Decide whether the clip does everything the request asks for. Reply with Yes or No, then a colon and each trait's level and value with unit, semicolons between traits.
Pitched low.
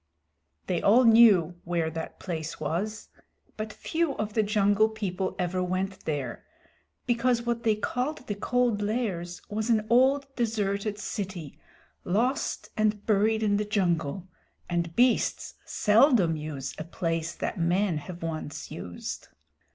No: high, 205 Hz